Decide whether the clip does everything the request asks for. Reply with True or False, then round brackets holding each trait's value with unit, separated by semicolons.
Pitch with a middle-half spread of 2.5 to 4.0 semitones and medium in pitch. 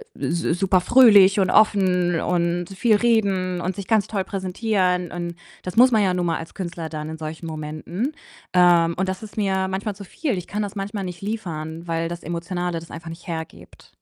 True (2.9 semitones; 180 Hz)